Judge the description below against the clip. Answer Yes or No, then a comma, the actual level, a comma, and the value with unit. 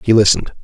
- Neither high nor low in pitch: No, low, 105 Hz